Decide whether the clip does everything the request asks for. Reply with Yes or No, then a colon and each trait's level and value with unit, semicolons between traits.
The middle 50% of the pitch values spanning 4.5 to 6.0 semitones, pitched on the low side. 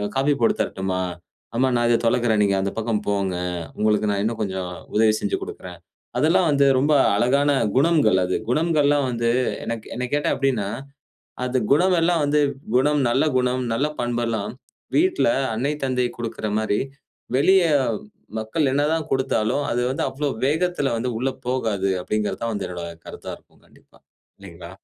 Yes: average, 5.2 semitones; low, 125 Hz